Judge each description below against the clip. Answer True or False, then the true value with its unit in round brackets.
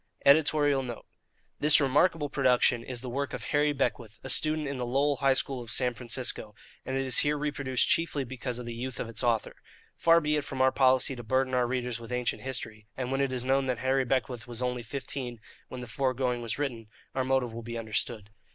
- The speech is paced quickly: True (225 wpm)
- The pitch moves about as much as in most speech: False (2.3 semitones)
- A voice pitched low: True (130 Hz)